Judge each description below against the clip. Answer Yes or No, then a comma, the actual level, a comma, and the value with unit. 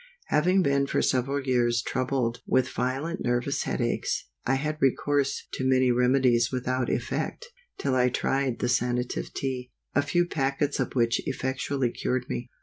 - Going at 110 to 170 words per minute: Yes, average, 155 wpm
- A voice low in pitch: Yes, low, 130 Hz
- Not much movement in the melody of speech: Yes, narrow, 1.9 semitones